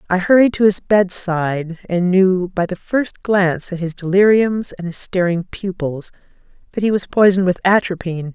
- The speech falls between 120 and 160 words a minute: No, average, 180 wpm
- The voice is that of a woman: Yes, female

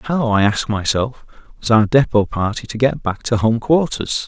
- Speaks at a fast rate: No, average, 195 wpm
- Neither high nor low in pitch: No, low, 115 Hz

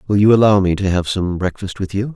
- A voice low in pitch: Yes, low, 100 Hz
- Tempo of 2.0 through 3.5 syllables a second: No, 6.0 syllables/s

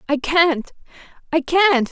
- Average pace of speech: No, slow, 125 wpm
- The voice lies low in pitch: No, very high, 310 Hz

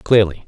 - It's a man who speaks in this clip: Yes, male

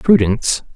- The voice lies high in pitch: No, low, 130 Hz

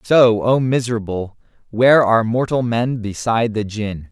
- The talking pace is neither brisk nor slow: Yes, average, 145 wpm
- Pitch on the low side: Yes, low, 115 Hz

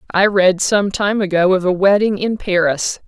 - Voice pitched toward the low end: No, high, 190 Hz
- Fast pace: No, average, 195 wpm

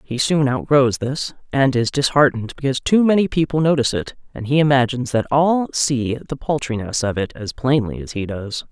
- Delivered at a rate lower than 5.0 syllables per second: No, 5.5 syllables/s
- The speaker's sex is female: Yes, female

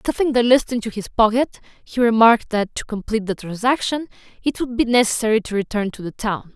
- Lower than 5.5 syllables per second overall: No, 6.0 syllables/s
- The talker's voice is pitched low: No, high, 225 Hz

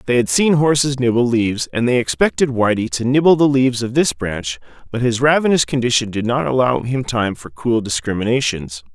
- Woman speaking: No, male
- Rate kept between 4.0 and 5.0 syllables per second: No, 5.5 syllables/s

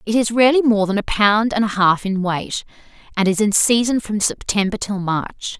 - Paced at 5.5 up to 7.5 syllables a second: No, 5.0 syllables/s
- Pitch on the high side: Yes, high, 210 Hz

